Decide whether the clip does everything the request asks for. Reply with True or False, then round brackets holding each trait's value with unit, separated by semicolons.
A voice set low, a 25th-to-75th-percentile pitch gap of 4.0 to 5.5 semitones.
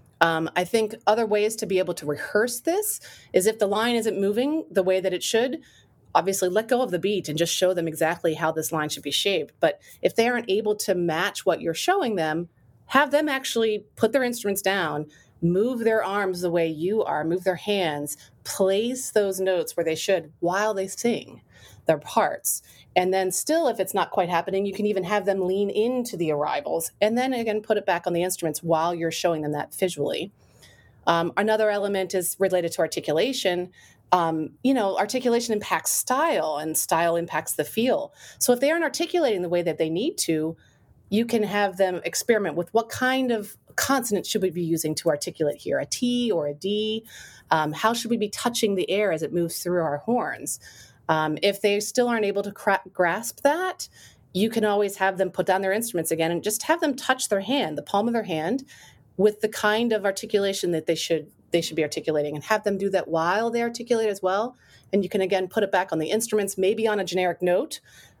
False (195 Hz; 4.5 semitones)